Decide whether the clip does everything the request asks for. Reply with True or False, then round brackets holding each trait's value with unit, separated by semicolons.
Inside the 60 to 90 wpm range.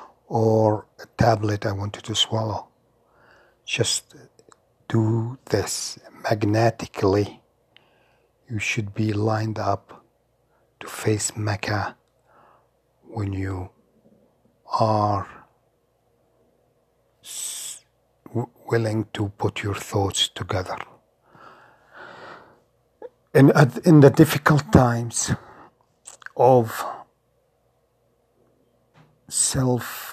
True (80 wpm)